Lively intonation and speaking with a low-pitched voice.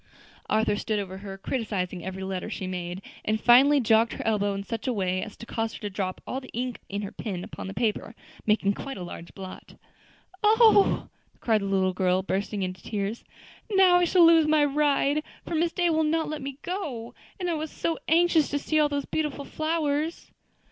No: wide, 7.8 semitones; high, 230 Hz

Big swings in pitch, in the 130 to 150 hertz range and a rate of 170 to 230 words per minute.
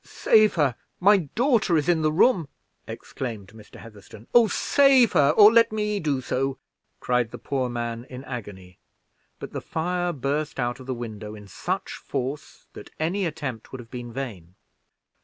Yes: wide, 7.0 semitones; low, 135 Hz; average, 175 wpm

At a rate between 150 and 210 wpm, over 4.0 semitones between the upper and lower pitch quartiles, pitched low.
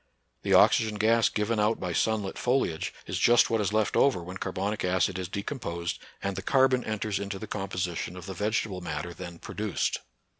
No: average, 190 wpm; average, 3.1 semitones; low, 100 Hz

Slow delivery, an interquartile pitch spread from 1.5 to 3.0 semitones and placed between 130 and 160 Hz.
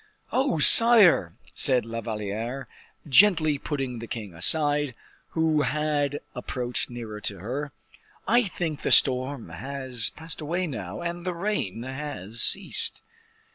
No: slow, 130 wpm; wide, 5.6 semitones; medium, 140 Hz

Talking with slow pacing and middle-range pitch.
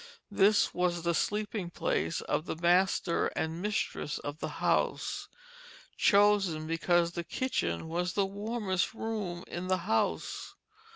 Yes: slow, 130 wpm; medium, 180 Hz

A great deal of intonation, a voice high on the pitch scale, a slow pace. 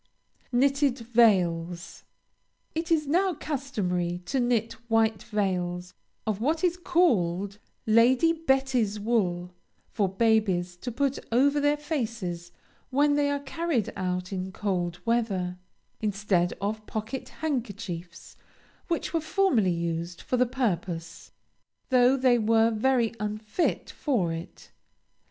Yes: wide, 6.6 semitones; high, 225 Hz; slow, 120 wpm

